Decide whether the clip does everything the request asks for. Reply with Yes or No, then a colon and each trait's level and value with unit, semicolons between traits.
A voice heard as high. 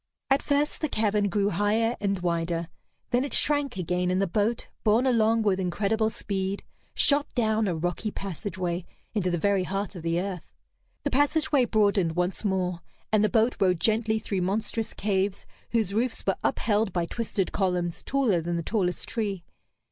Yes: high, 200 Hz